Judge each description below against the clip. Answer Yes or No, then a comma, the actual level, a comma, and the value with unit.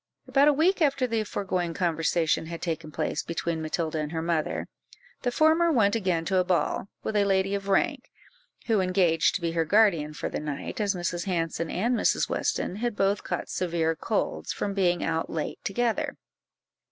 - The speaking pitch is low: No, medium, 185 Hz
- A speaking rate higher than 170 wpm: Yes, average, 185 wpm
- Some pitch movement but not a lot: Yes, average, 4.2 semitones